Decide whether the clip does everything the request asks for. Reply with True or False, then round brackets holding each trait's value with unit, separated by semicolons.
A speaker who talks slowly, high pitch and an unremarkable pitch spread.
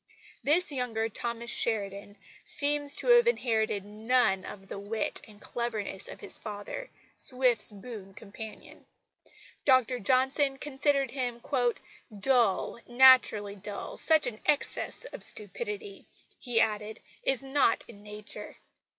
True (120 wpm; 235 Hz; 4.4 semitones)